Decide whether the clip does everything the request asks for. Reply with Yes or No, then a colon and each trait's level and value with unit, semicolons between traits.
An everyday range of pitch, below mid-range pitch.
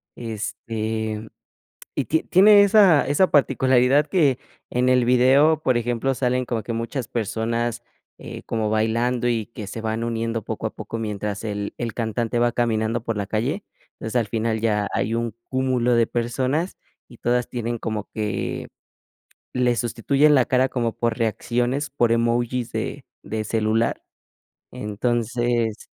No: narrow, 2.2 semitones; low, 120 Hz